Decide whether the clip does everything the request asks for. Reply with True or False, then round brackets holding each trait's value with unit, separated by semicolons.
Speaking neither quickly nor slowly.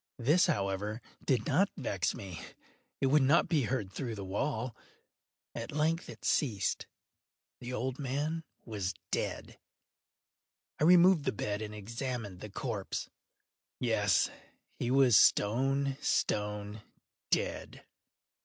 False (120 wpm)